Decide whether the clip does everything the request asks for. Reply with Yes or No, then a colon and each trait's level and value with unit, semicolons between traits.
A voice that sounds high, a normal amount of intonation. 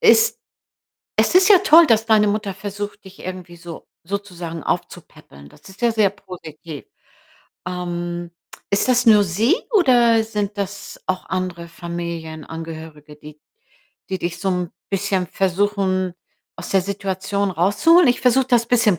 Yes: high, 195 Hz; average, 3.8 semitones